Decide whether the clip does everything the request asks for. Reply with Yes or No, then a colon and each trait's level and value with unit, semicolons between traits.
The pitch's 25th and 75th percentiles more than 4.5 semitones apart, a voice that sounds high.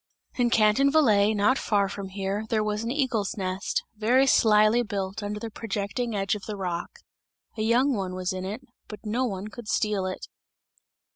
No: average, 2.7 semitones; high, 210 Hz